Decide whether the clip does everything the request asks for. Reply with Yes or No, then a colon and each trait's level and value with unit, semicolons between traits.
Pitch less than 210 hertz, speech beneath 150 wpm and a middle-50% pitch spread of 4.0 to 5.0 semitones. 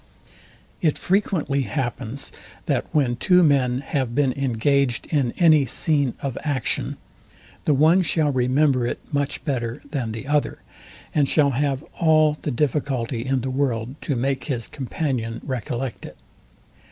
No: low, 135 Hz; average, 140 wpm; average, 3.2 semitones